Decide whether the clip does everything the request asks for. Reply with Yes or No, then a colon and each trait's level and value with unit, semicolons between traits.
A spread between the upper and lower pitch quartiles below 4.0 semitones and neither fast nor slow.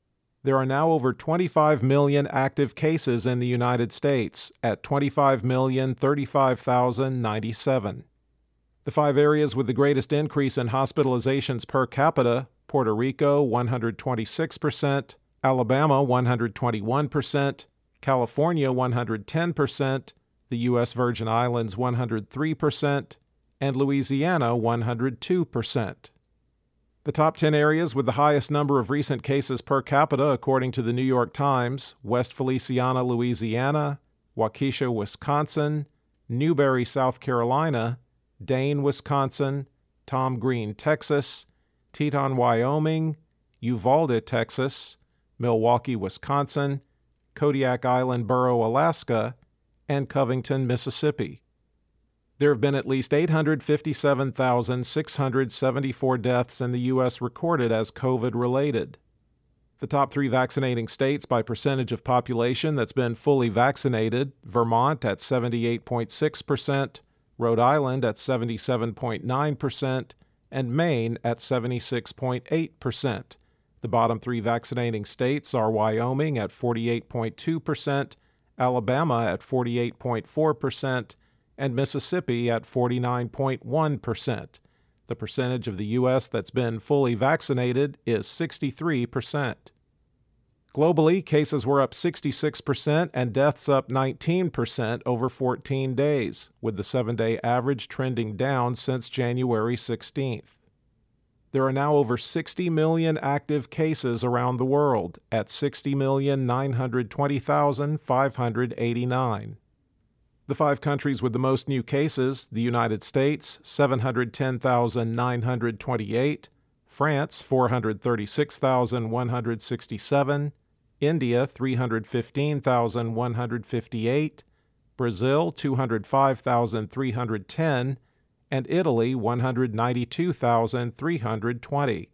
No: average, 2.9 semitones; slow, 95 wpm